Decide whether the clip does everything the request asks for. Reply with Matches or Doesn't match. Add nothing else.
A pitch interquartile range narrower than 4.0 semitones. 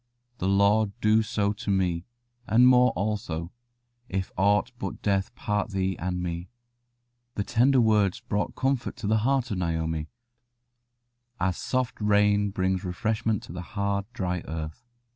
Matches